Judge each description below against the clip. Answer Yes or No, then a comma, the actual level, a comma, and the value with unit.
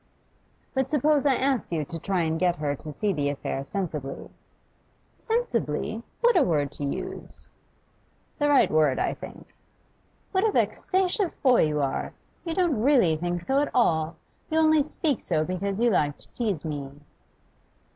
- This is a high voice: Yes, high, 195 Hz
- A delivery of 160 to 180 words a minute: Yes, average, 165 wpm